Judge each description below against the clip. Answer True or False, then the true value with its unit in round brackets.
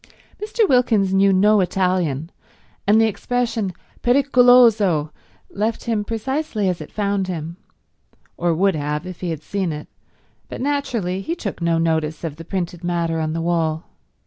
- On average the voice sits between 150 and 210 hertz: True (190 Hz)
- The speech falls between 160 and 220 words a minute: False (150 wpm)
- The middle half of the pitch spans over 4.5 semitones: True (5.2 semitones)